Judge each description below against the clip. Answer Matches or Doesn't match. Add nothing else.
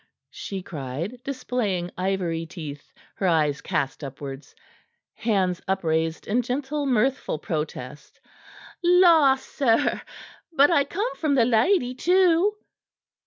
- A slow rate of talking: Matches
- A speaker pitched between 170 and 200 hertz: Doesn't match